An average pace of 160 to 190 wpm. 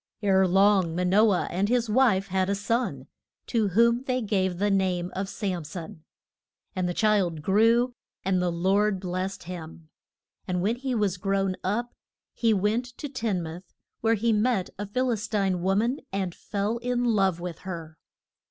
Yes: average, 180 wpm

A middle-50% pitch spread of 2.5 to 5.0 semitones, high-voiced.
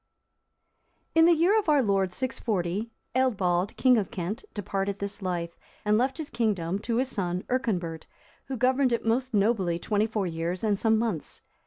No: wide, 5.4 semitones; high, 210 Hz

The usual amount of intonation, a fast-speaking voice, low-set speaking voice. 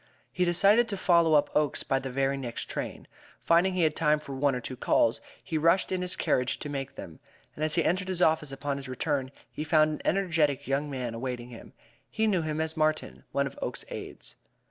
No: average, 3.8 semitones; fast, 220 wpm; medium, 150 Hz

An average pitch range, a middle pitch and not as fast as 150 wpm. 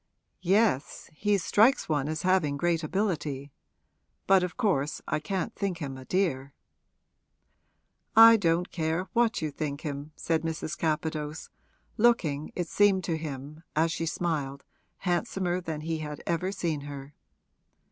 Yes: average, 4.0 semitones; medium, 165 Hz; average, 140 wpm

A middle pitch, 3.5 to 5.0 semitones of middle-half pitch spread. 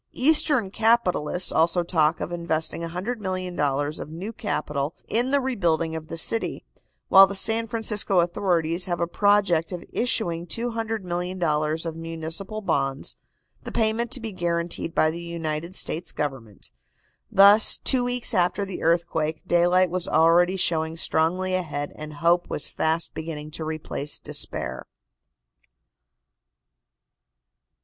Yes: medium, 175 Hz; average, 3.8 semitones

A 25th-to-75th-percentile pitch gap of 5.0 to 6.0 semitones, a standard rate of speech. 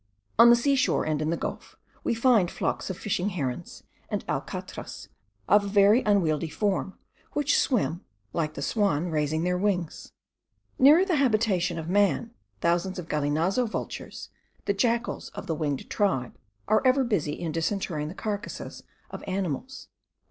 Yes: wide, 5.6 semitones; average, 155 wpm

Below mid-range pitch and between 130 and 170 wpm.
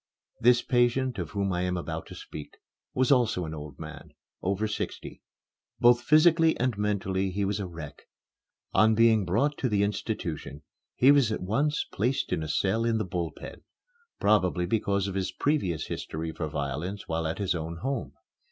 No: low, 100 Hz; average, 180 wpm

